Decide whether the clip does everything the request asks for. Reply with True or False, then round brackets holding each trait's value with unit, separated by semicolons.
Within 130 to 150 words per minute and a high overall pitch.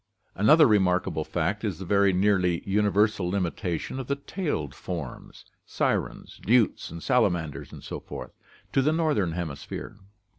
False (140 wpm; 95 Hz)